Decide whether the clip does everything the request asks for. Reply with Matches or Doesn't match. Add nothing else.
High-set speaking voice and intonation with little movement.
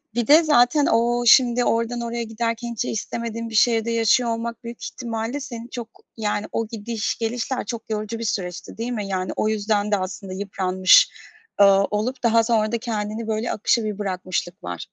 Matches